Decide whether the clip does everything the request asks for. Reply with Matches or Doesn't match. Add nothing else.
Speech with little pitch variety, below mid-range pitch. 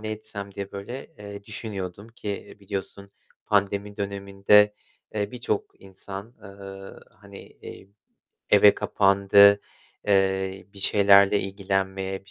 Matches